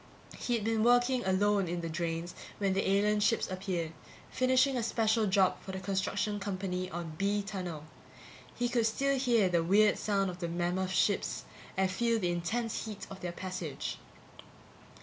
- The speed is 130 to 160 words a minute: No, average, 170 wpm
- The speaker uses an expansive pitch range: No, average, 3.5 semitones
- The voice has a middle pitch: No, high, 195 Hz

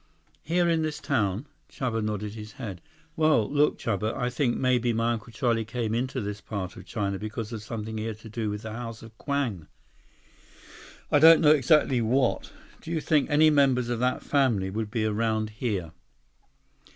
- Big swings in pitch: No, average, 4.0 semitones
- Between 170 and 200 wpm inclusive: Yes, average, 185 wpm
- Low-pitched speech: Yes, low, 115 Hz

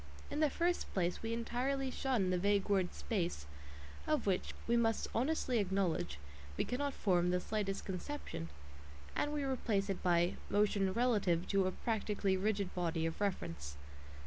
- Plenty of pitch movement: No, average, 5.0 semitones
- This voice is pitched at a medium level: No, high, 200 Hz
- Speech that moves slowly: No, average, 155 wpm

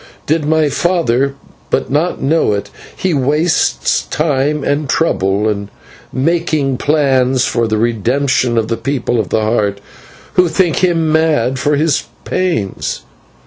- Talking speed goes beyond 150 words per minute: No, slow, 135 wpm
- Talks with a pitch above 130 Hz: Yes, medium, 140 Hz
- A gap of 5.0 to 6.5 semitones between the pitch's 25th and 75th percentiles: Yes, average, 5.3 semitones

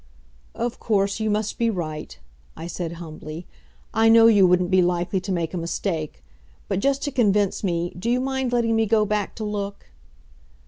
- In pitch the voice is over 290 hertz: No, high, 200 Hz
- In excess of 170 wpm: Yes, average, 185 wpm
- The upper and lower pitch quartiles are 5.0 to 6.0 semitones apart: No, average, 4.3 semitones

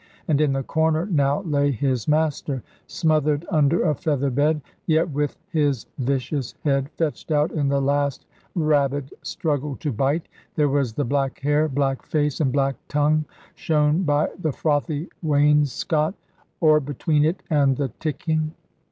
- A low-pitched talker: No, medium, 145 Hz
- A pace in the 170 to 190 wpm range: No, average, 150 wpm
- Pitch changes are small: Yes, narrow, 1.9 semitones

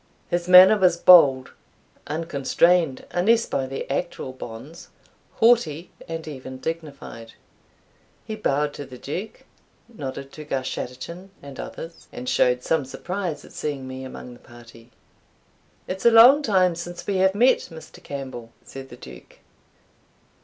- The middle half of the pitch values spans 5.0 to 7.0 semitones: Yes, wide, 5.6 semitones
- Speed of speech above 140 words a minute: No, slow, 135 wpm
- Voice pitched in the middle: Yes, medium, 155 Hz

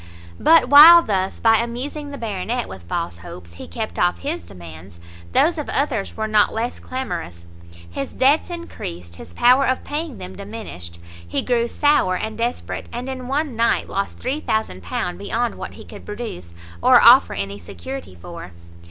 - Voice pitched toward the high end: Yes, high, 220 Hz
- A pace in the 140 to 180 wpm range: Yes, average, 165 wpm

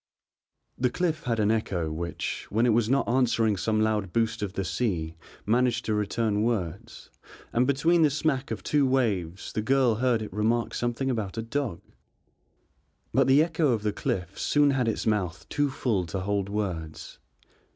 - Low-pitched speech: Yes, low, 115 Hz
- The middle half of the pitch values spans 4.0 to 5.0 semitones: Yes, average, 4.3 semitones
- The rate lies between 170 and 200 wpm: Yes, average, 175 wpm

